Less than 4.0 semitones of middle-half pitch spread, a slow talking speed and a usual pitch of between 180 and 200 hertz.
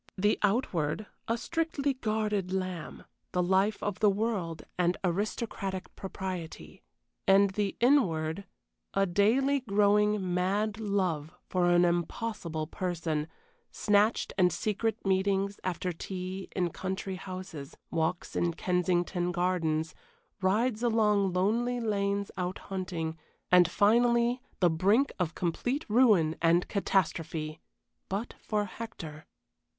Yes: average, 3.2 semitones; slow, 115 wpm; high, 190 Hz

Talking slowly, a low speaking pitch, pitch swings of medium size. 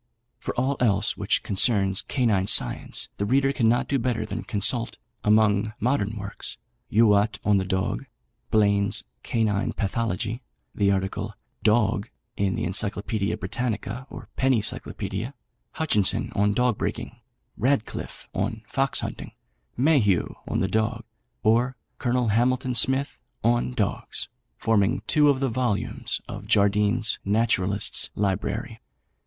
Yes: slow, 125 wpm; low, 110 Hz; average, 3.4 semitones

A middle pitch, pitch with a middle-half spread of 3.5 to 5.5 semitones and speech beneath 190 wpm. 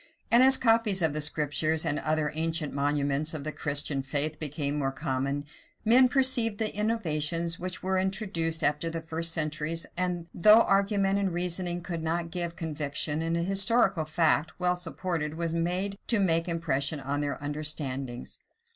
Yes: medium, 165 Hz; average, 3.8 semitones; average, 160 wpm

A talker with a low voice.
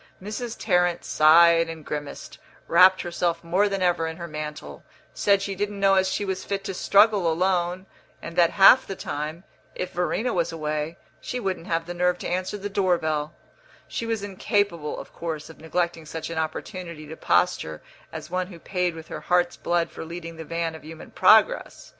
No: medium, 175 Hz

